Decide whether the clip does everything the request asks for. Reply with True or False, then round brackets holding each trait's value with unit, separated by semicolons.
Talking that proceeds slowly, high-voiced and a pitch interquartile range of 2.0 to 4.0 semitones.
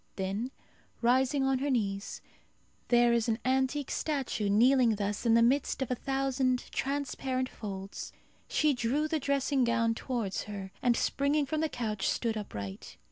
False (155 wpm; 245 Hz; 3.7 semitones)